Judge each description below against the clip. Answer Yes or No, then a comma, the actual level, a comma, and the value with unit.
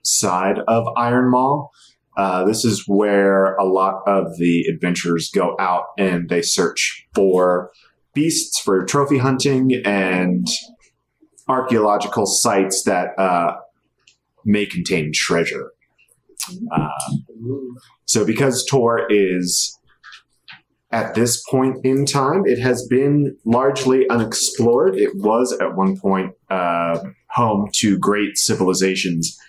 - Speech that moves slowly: Yes, slow, 115 wpm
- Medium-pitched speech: No, low, 105 Hz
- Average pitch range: No, wide, 5.8 semitones